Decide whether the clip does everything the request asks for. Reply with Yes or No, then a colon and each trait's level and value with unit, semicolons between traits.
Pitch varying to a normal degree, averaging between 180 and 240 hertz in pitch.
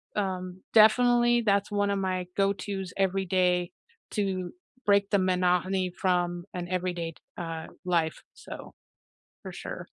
No: narrow, 2.0 semitones; medium, 185 Hz